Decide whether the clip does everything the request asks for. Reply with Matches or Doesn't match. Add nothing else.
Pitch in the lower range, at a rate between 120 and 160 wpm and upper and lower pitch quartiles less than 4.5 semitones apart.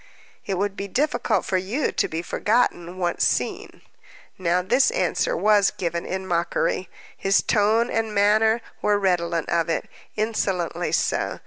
Doesn't match